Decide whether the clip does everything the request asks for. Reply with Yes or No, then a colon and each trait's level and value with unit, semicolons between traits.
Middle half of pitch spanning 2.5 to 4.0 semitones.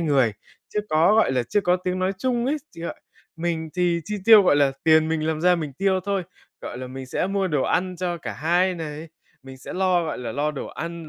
Yes: average, 3.5 semitones